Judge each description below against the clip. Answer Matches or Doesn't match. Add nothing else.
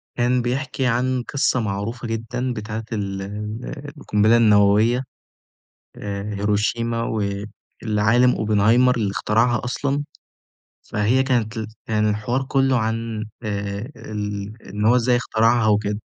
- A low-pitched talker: Matches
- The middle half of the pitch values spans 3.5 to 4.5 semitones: Doesn't match